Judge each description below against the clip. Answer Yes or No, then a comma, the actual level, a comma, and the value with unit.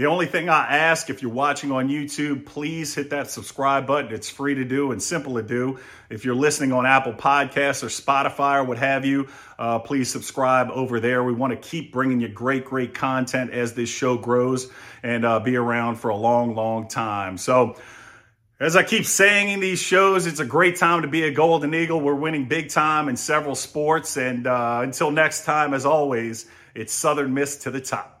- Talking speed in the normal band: No, fast, 210 wpm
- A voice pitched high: No, low, 135 Hz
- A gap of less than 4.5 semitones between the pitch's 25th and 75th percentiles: Yes, average, 3.5 semitones